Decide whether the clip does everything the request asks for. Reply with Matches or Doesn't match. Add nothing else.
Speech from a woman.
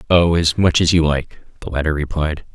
Doesn't match